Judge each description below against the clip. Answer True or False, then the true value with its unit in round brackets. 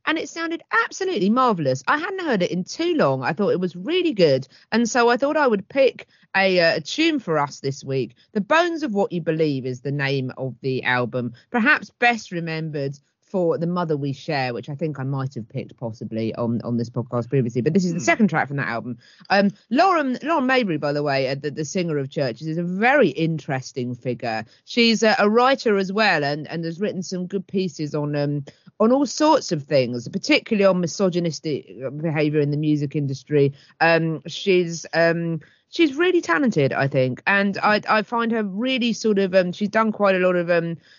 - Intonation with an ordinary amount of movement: False (7.7 semitones)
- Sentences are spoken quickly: True (210 wpm)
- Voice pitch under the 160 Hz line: False (170 Hz)